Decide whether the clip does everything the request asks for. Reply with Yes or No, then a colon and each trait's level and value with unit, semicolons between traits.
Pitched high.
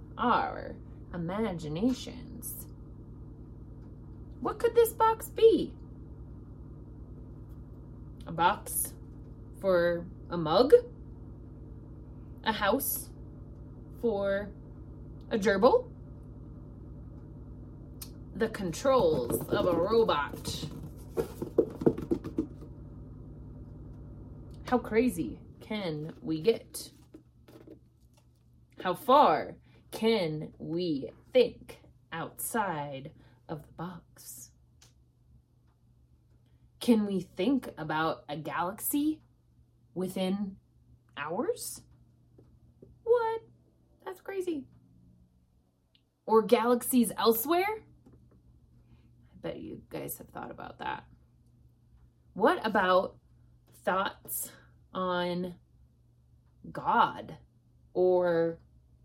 No: low, 135 Hz